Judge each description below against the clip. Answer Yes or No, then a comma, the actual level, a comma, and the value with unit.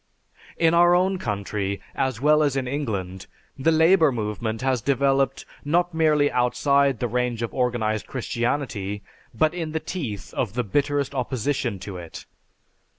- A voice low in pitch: Yes, low, 130 Hz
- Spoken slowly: No, average, 150 wpm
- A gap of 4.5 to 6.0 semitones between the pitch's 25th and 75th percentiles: Yes, average, 5.0 semitones